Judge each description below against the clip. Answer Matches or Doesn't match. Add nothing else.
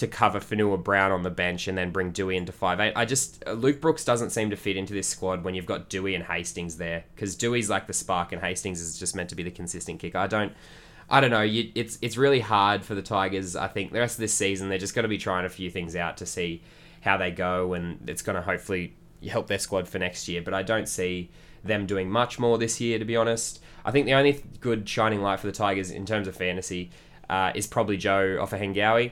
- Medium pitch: Doesn't match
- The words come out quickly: Matches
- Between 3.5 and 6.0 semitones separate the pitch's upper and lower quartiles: Matches